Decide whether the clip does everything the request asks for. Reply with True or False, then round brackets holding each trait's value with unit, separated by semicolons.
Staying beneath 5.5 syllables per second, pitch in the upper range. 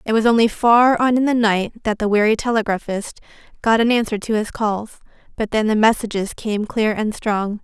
True (5.1 syllables/s; 220 Hz)